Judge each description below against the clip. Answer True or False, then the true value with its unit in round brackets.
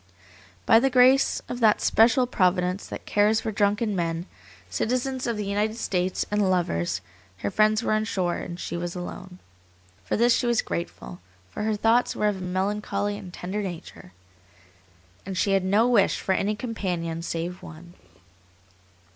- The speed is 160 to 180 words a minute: True (165 wpm)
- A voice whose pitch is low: False (200 Hz)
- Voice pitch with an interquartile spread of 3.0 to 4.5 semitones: True (3.6 semitones)